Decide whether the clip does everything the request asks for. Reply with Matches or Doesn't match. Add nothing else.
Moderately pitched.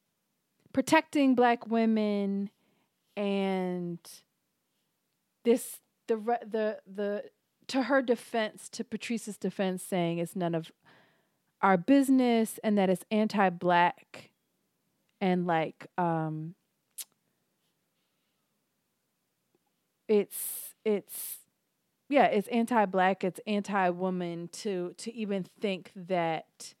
Doesn't match